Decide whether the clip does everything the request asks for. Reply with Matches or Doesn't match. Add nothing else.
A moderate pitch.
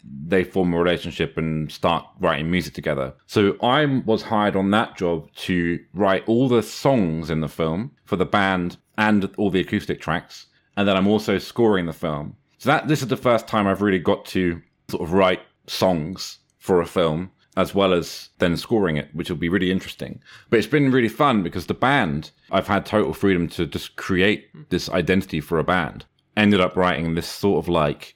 Doesn't match